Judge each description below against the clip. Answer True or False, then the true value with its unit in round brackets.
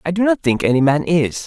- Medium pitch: True (160 Hz)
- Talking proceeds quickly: True (285 wpm)